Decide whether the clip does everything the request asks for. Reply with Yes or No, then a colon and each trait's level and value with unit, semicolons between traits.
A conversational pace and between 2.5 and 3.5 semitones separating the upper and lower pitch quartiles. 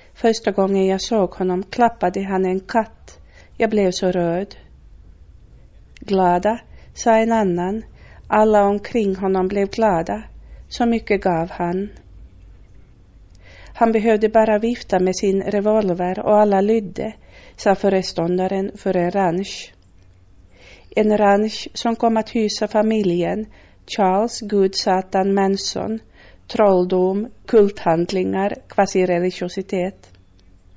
No: slow, 105 wpm; average, 3.2 semitones